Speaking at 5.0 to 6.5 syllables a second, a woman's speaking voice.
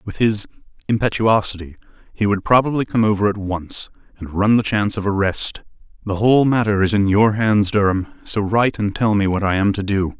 No: 5.6 syllables/s; male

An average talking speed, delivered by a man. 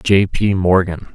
Yes: average, 155 wpm; male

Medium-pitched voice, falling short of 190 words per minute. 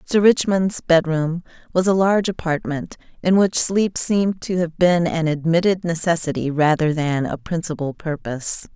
Yes: medium, 170 Hz; average, 150 wpm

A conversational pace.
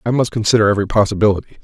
Yes: average, 185 wpm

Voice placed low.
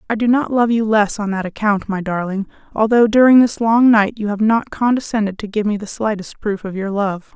No: high, 215 Hz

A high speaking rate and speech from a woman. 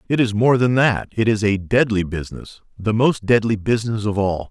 No: fast, 215 wpm; male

